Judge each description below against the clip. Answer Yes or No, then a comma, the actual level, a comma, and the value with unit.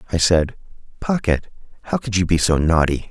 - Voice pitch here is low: Yes, very low, 90 Hz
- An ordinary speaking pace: Yes, average, 175 wpm